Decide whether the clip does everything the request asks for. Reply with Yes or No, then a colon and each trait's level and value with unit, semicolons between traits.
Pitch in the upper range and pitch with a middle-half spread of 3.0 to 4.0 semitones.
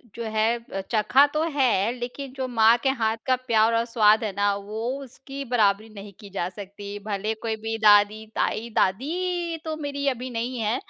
Yes: high, 230 Hz; average, 3.6 semitones